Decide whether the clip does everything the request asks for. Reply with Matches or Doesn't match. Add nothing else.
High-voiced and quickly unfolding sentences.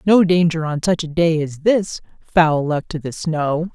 Doesn't match